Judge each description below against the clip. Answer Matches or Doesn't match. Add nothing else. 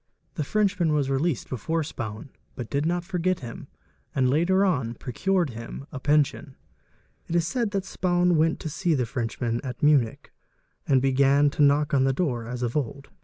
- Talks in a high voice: Doesn't match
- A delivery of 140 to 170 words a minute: Doesn't match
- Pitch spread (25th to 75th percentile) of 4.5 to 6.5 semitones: Matches